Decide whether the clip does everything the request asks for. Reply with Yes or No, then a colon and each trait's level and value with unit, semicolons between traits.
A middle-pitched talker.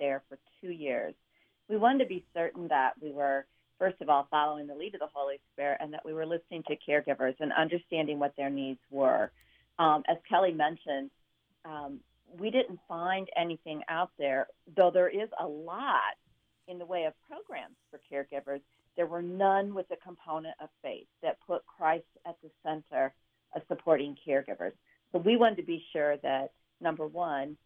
Yes: medium, 155 Hz